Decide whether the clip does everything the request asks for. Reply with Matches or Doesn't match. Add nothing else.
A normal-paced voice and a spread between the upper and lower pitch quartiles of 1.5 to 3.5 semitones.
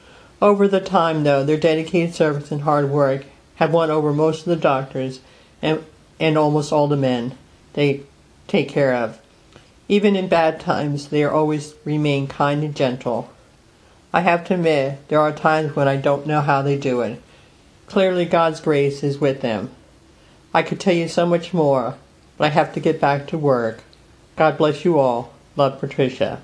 Matches